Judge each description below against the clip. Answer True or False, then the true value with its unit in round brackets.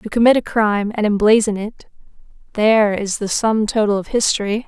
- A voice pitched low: False (215 Hz)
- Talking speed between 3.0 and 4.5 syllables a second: False (5.5 syllables/s)